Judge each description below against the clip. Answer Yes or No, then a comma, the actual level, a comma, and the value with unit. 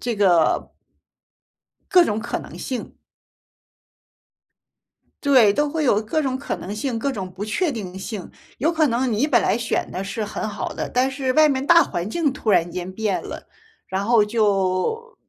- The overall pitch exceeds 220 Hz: Yes, high, 230 Hz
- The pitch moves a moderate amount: No, wide, 5.8 semitones